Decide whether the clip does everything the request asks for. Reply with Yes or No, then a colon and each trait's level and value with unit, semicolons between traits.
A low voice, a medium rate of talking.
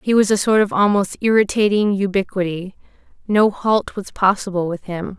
No: high, 195 Hz; average, 160 wpm